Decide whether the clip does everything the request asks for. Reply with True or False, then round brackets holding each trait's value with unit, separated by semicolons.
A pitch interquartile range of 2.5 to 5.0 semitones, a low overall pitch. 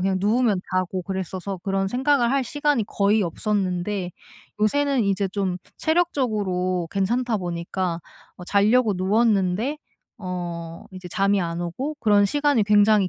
False (4.2 semitones; 200 Hz)